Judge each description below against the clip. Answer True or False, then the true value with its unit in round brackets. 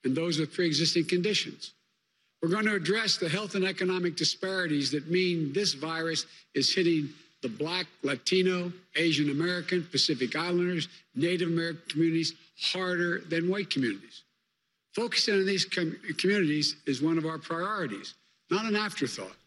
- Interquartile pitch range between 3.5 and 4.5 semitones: False (2.5 semitones)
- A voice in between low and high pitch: True (170 Hz)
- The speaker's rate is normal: True (150 wpm)